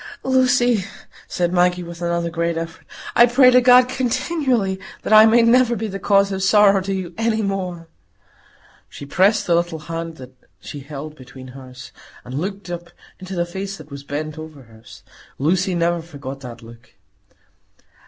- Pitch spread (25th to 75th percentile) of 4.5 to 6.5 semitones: Yes, average, 5.3 semitones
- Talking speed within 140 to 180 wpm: Yes, average, 170 wpm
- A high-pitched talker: No, medium, 175 Hz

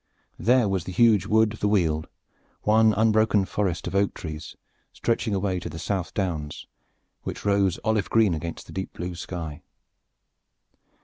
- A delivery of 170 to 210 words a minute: No, average, 160 wpm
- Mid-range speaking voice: No, low, 100 Hz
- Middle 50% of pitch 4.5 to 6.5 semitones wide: No, average, 3.7 semitones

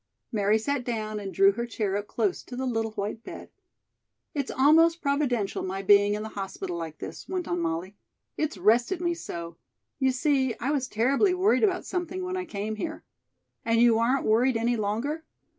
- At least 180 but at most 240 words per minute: Yes, average, 190 wpm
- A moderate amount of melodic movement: No, wide, 6.1 semitones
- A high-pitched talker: Yes, high, 235 Hz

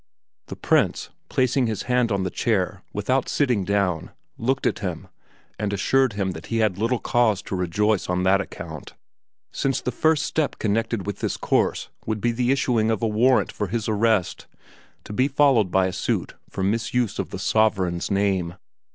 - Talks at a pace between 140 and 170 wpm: No, average, 180 wpm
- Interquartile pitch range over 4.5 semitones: No, average, 4.1 semitones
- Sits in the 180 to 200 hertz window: No, low, 110 Hz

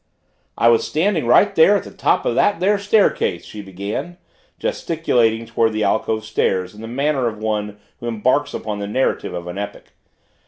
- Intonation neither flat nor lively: No, wide, 7.0 semitones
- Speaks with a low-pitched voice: Yes, low, 115 Hz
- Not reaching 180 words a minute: No, average, 185 wpm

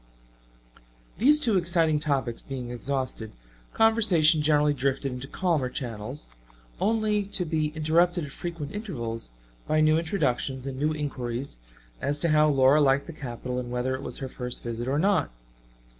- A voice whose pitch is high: No, medium, 145 Hz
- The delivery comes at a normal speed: Yes, average, 155 wpm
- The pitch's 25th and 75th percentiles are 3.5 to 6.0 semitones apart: Yes, average, 4.6 semitones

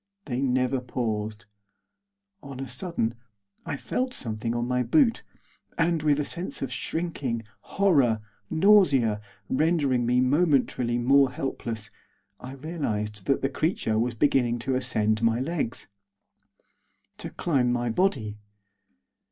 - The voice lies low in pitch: Yes, low, 130 Hz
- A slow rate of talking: Yes, slow, 125 wpm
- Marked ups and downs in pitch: No, average, 4.4 semitones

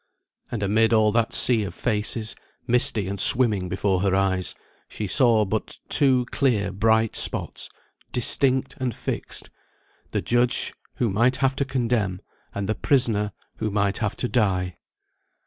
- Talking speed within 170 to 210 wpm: No, average, 145 wpm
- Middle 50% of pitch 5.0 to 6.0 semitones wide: No, average, 3.7 semitones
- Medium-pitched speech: No, low, 110 Hz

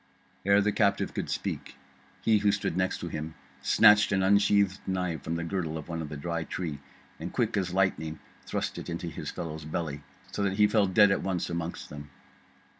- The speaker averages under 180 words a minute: No, average, 195 wpm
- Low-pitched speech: Yes, very low, 90 Hz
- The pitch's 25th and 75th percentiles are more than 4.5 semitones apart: No, average, 3.8 semitones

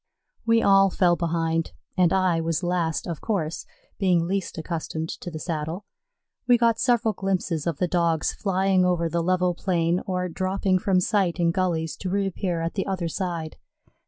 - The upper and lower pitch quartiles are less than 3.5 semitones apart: Yes, narrow, 2.4 semitones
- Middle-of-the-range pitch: Yes, medium, 180 Hz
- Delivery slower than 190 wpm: Yes, average, 170 wpm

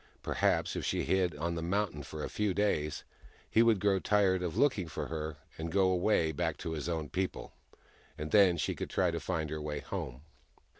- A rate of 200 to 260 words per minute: Yes, fast, 205 wpm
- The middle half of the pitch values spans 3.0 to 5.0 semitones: Yes, average, 3.9 semitones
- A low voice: Yes, very low, 85 Hz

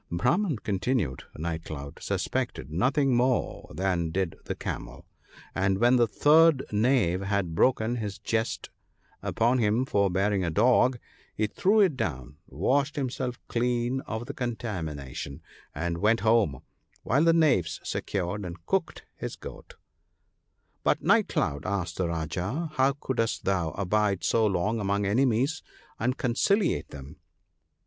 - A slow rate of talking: No, average, 145 wpm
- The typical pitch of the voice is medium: No, low, 105 Hz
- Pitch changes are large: Yes, wide, 6.3 semitones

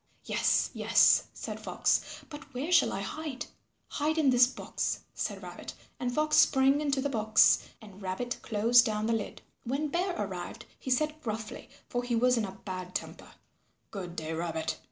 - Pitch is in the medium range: No, high, 245 Hz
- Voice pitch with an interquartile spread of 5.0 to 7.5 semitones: Yes, average, 5.3 semitones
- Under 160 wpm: No, average, 175 wpm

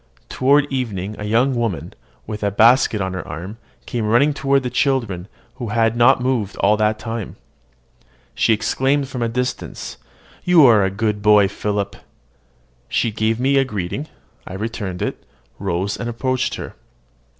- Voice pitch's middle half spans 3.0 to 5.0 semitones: Yes, average, 3.8 semitones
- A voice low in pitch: Yes, low, 115 Hz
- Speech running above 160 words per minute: No, average, 155 wpm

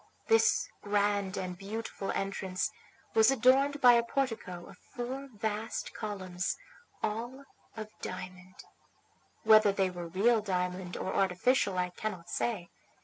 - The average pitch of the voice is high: Yes, high, 205 Hz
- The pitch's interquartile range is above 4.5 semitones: No, average, 4.1 semitones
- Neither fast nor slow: No, slow, 125 wpm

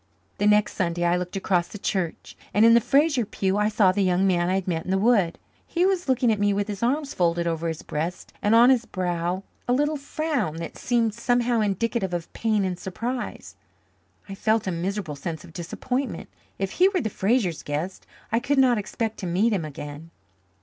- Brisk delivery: Yes, fast, 210 wpm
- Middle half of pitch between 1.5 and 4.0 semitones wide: No, average, 5.1 semitones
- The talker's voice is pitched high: Yes, high, 200 Hz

